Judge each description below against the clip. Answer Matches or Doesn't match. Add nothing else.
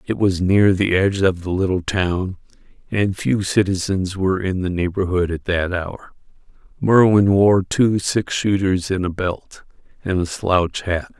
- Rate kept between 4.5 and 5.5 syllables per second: Doesn't match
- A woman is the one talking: Doesn't match